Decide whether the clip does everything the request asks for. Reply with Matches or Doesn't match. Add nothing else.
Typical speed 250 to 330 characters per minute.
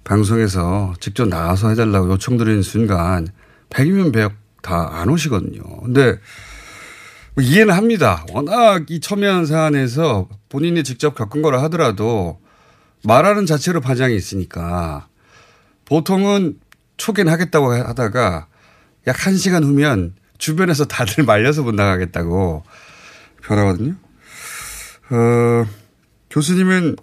Matches